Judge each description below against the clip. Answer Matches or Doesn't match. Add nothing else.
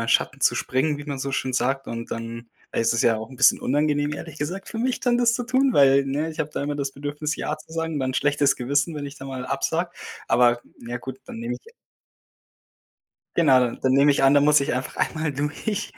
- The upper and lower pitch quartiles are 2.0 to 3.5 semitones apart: Matches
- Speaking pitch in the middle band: Matches